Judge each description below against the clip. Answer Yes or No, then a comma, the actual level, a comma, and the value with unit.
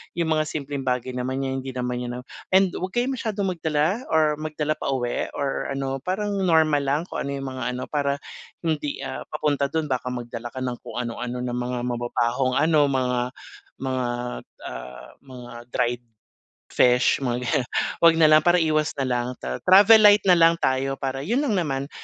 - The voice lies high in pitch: No, medium, 140 Hz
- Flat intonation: No, average, 4.1 semitones